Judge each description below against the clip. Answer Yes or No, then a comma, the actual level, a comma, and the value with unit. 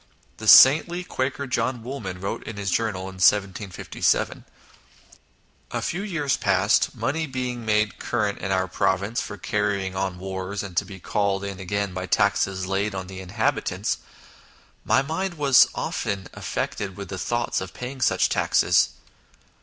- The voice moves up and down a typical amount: Yes, average, 4.6 semitones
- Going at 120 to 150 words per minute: No, average, 165 wpm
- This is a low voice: Yes, low, 100 Hz